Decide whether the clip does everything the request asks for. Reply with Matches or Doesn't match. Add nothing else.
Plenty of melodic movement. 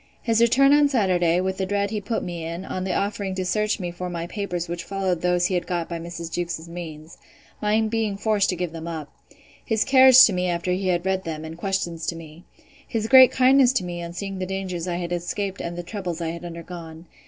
Doesn't match